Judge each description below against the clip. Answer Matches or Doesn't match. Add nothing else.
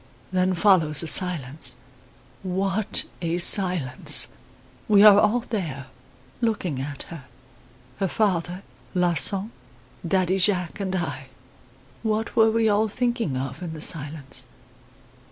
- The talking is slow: Matches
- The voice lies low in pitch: Doesn't match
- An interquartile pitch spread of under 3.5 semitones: Doesn't match